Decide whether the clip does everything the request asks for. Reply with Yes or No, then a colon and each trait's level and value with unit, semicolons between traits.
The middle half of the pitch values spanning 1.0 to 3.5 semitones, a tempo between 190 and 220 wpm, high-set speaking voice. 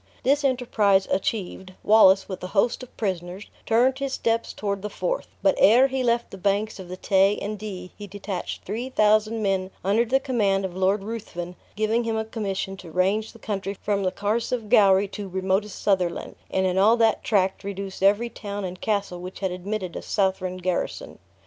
Yes: average, 2.7 semitones; average, 195 wpm; high, 200 Hz